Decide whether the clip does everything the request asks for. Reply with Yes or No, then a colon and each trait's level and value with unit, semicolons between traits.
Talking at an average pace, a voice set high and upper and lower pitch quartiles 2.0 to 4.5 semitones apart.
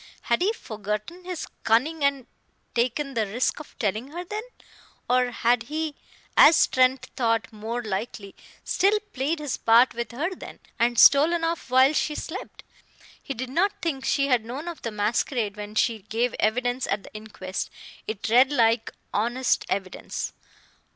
No: average, 160 wpm; high, 245 Hz; average, 4.9 semitones